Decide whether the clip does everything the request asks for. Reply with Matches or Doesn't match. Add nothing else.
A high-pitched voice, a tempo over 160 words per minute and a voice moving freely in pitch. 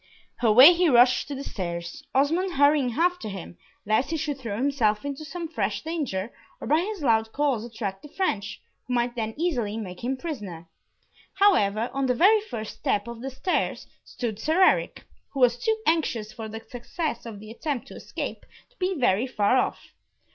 Matches